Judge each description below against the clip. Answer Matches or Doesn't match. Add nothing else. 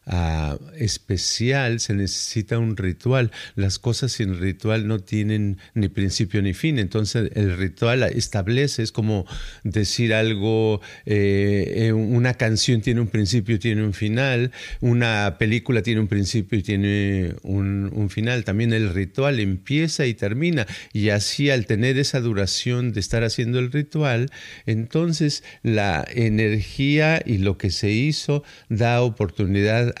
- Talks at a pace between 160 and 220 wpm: Doesn't match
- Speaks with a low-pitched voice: Matches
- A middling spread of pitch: Matches